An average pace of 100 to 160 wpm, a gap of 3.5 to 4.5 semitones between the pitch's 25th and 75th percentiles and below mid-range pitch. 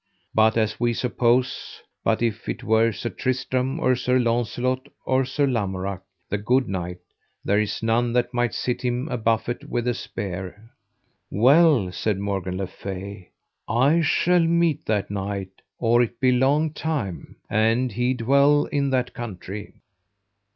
Yes: average, 150 wpm; average, 4.0 semitones; low, 120 Hz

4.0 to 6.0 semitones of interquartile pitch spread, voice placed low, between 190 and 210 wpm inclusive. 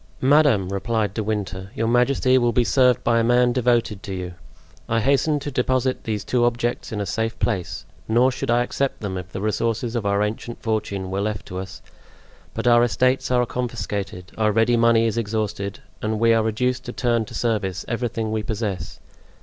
No: average, 2.8 semitones; low, 115 Hz; average, 195 wpm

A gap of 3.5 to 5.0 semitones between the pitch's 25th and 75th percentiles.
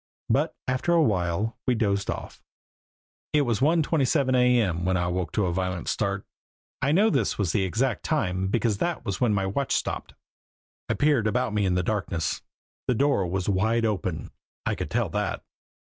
No: wide, 5.5 semitones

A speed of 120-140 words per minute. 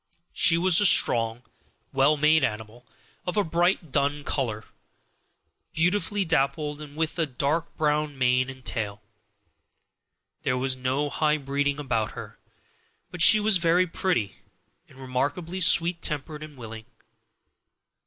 Yes: slow, 135 wpm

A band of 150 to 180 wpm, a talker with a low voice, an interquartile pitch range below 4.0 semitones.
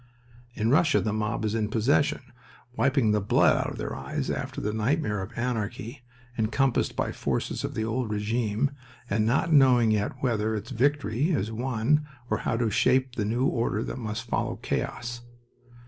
Yes: average, 175 wpm; low, 115 Hz; average, 3.3 semitones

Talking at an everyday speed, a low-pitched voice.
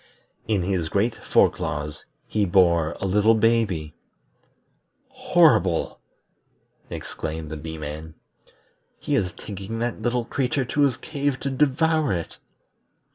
No: slow, 125 wpm; low, 100 Hz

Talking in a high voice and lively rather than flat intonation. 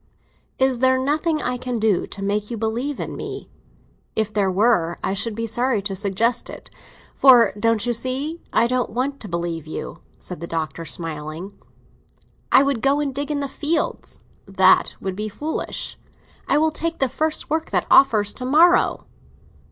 Yes: high, 235 Hz; wide, 5.8 semitones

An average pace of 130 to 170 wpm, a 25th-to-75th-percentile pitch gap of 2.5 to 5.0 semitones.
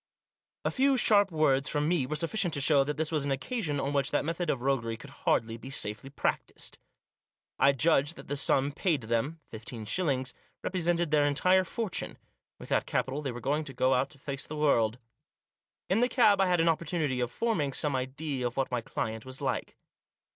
No: fast, 205 wpm; average, 4.2 semitones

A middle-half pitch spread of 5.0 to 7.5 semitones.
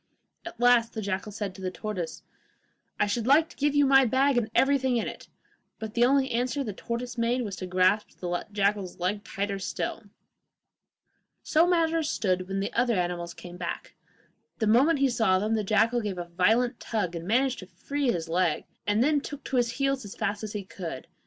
Yes: average, 5.3 semitones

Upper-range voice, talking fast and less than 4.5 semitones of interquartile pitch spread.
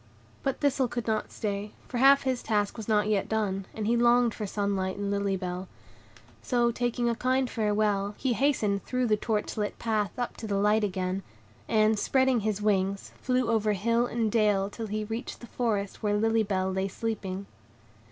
No: high, 215 Hz; average, 190 wpm; average, 2.9 semitones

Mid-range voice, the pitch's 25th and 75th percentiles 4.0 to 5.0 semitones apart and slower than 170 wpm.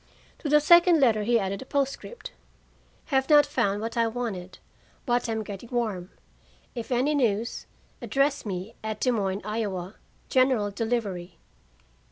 No: high, 230 Hz; average, 4.7 semitones; average, 145 wpm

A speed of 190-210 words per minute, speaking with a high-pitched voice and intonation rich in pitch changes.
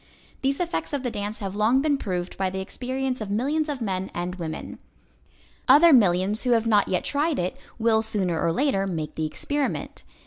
Yes: average, 195 wpm; high, 220 Hz; wide, 6.2 semitones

